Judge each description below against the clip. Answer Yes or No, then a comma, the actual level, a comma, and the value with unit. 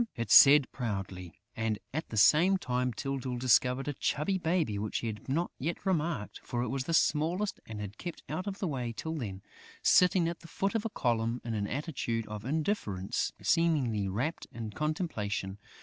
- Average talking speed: Yes, average, 185 wpm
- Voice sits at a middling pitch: No, low, 130 Hz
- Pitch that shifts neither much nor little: No, wide, 6.9 semitones